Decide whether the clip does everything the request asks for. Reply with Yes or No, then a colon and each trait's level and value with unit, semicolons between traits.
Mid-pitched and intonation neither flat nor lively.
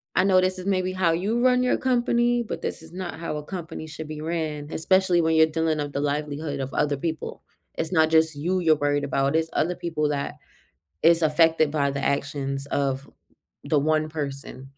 Yes: medium, 160 Hz; average, 3.2 semitones